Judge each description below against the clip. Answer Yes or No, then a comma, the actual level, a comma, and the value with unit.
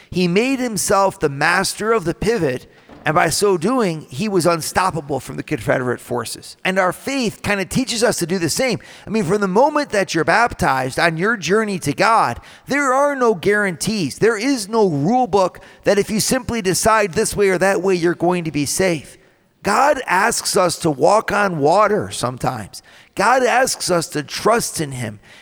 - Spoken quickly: No, average, 195 wpm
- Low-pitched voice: No, high, 190 Hz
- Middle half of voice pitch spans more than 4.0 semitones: Yes, average, 4.6 semitones